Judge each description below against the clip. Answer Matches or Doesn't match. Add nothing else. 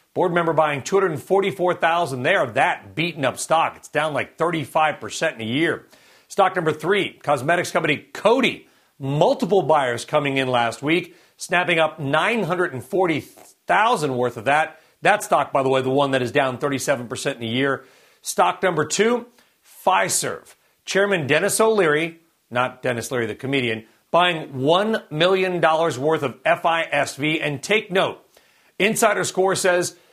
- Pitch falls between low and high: Matches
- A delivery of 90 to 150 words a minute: Matches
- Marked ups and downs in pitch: Doesn't match